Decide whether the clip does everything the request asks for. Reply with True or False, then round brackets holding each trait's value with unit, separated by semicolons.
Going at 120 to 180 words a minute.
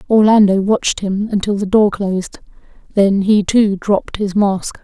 True (160 wpm)